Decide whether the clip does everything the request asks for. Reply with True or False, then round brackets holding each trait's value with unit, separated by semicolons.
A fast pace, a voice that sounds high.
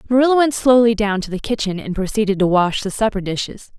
True (220 wpm; 215 Hz)